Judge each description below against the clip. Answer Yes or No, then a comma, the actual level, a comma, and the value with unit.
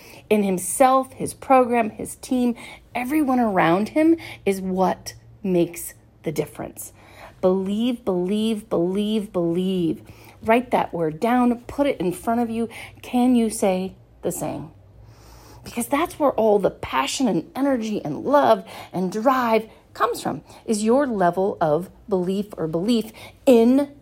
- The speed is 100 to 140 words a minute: Yes, slow, 135 wpm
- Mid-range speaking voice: No, high, 215 Hz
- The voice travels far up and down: Yes, wide, 5.8 semitones